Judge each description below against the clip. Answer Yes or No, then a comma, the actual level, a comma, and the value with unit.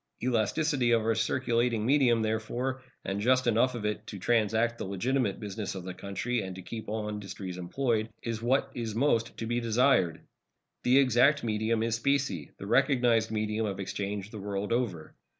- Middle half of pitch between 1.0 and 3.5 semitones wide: Yes, average, 2.9 semitones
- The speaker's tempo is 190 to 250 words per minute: No, average, 175 wpm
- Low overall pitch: Yes, low, 115 Hz